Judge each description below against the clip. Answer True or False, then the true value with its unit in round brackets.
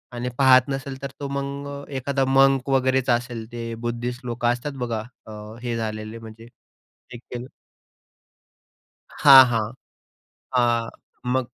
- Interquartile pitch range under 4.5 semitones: True (2.4 semitones)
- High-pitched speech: False (125 Hz)